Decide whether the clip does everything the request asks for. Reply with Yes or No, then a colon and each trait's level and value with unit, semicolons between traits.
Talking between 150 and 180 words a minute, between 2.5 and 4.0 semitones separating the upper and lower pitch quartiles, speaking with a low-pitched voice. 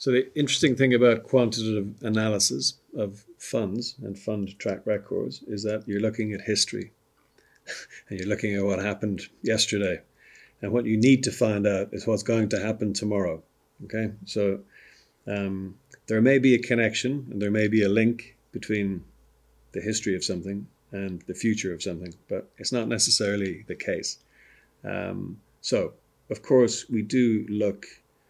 Yes: average, 160 wpm; average, 2.8 semitones; low, 105 Hz